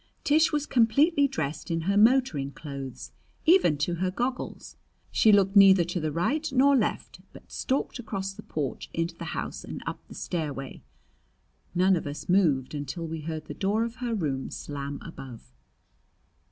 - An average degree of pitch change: No, wide, 7.7 semitones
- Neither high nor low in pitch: Yes, medium, 180 Hz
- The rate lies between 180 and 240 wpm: No, average, 165 wpm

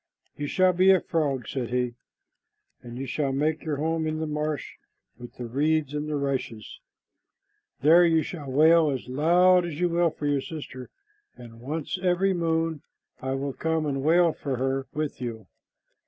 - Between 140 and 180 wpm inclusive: Yes, average, 175 wpm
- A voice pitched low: No, medium, 150 Hz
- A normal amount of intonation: Yes, average, 3.4 semitones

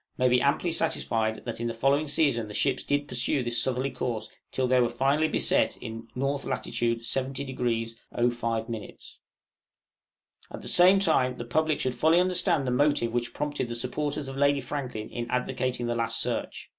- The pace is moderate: Yes, average, 175 wpm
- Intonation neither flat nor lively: Yes, average, 3.2 semitones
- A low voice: Yes, low, 125 Hz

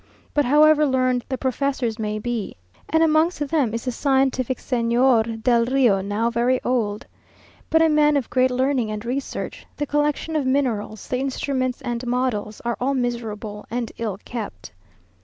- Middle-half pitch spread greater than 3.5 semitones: No, average, 3.2 semitones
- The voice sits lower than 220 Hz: No, very high, 250 Hz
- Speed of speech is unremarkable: Yes, average, 160 wpm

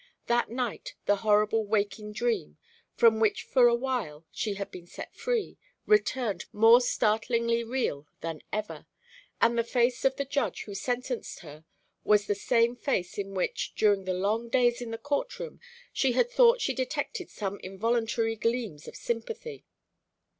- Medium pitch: No, high, 230 Hz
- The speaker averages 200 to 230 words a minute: No, average, 155 wpm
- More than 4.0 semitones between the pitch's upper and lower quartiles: No, average, 3.6 semitones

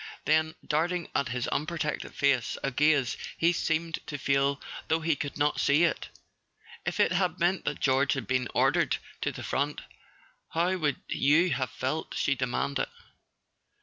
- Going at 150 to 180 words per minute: Yes, average, 160 wpm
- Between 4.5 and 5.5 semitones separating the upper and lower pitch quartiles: No, average, 3.1 semitones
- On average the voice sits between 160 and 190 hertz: No, medium, 150 Hz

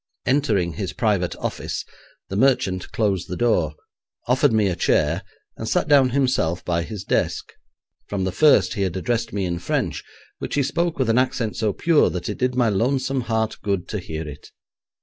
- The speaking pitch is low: Yes, low, 110 Hz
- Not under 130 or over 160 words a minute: No, average, 190 wpm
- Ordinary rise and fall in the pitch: No, wide, 5.7 semitones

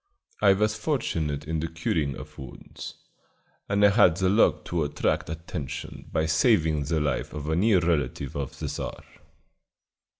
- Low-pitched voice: Yes, very low, 80 Hz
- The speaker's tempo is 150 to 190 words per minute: Yes, average, 160 wpm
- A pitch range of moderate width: Yes, average, 4.7 semitones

